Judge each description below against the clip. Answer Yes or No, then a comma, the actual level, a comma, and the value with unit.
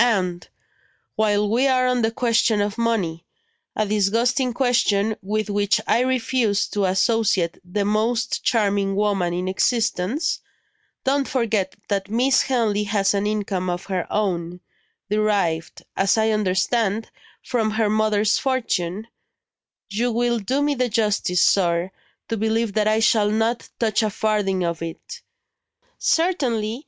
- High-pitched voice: Yes, high, 215 Hz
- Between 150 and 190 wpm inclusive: No, average, 140 wpm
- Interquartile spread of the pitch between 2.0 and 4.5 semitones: Yes, average, 2.9 semitones